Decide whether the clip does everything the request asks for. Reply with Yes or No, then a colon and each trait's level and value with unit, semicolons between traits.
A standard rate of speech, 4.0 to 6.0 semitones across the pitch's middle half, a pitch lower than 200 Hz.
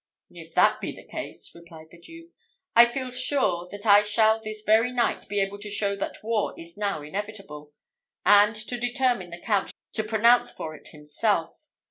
No: average, 180 wpm; average, 4.6 semitones; high, 210 Hz